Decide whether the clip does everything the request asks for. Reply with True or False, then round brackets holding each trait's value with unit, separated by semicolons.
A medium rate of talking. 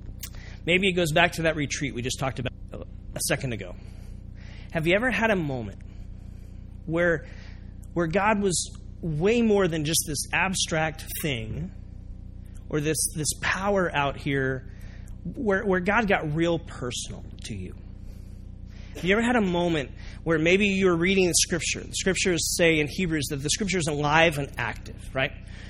True (165 wpm)